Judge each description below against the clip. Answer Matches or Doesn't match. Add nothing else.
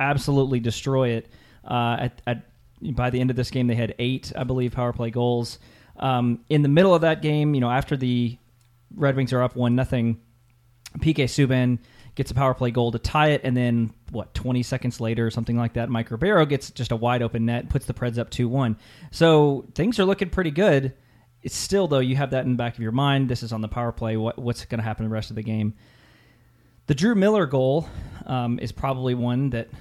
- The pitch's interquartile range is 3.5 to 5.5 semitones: Doesn't match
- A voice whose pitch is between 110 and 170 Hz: Matches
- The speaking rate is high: Matches